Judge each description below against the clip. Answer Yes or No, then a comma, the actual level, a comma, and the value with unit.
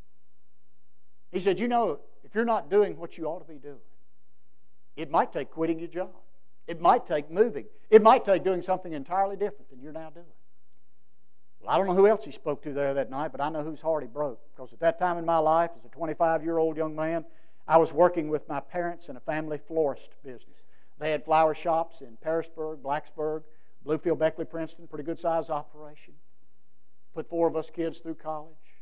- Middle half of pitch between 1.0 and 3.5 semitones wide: Yes, average, 3.0 semitones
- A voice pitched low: No, medium, 155 Hz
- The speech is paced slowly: No, average, 200 wpm